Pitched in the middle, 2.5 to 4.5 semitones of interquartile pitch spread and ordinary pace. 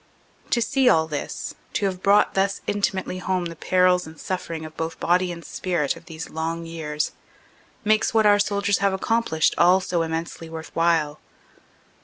Yes: medium, 175 Hz; average, 3.4 semitones; average, 170 wpm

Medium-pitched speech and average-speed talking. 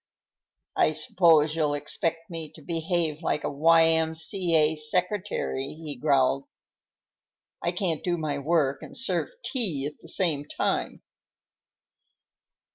No: medium, 160 Hz; slow, 120 wpm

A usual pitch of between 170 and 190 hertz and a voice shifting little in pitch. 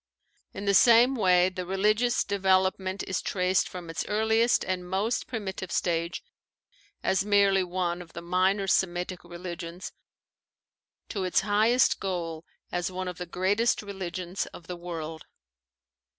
Yes: medium, 185 Hz; narrow, 2.2 semitones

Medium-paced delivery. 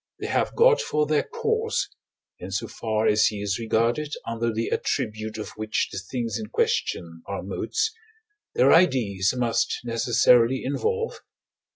Yes: average, 155 wpm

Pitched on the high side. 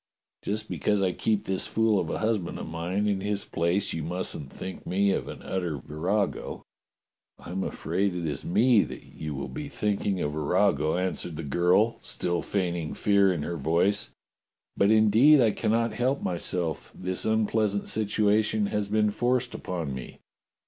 No: low, 100 Hz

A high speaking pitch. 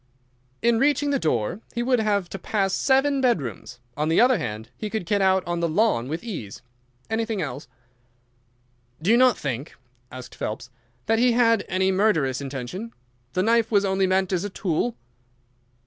Yes: high, 195 Hz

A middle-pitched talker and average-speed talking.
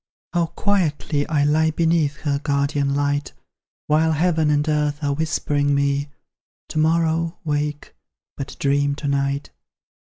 No: medium, 150 Hz; slow, 130 wpm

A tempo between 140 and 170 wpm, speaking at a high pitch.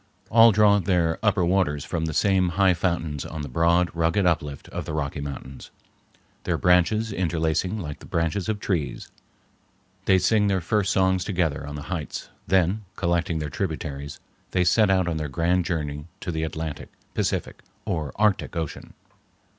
No: average, 165 wpm; very low, 85 Hz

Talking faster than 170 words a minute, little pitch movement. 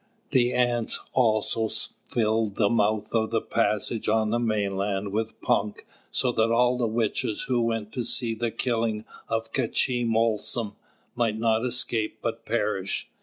No: average, 155 wpm; narrow, 1.7 semitones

